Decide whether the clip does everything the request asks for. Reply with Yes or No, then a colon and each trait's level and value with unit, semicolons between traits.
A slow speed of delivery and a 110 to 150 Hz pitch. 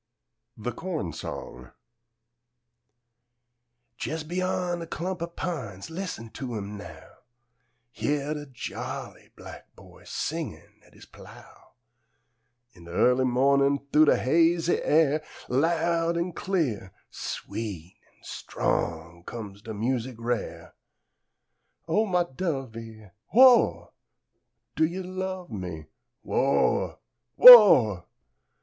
Yes: slow, 110 wpm; medium, 140 Hz